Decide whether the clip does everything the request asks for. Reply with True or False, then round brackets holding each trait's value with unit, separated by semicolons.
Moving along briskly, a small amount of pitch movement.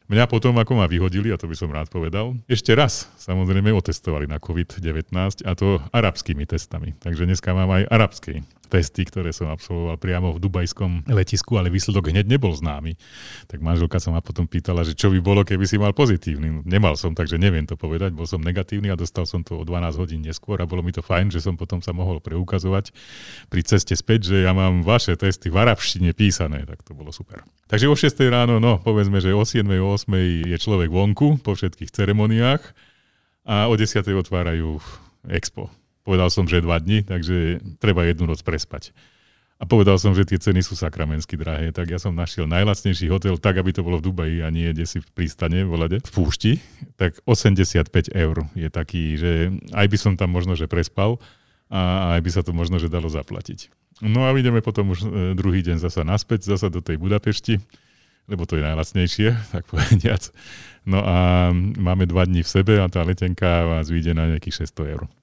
False (200 wpm; 3.2 semitones)